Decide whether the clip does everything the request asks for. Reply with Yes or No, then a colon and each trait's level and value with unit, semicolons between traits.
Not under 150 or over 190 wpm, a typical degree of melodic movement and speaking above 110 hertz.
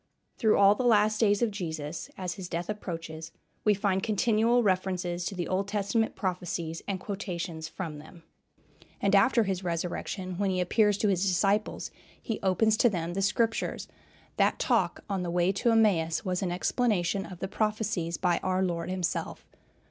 Yes: average, 170 wpm; average, 3.1 semitones; high, 190 Hz